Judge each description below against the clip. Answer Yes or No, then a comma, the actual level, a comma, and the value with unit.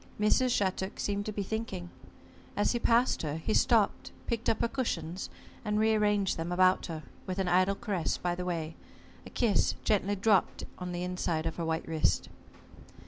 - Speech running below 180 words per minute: No, average, 185 wpm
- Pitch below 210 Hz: Yes, high, 190 Hz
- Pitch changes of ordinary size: Yes, average, 3.4 semitones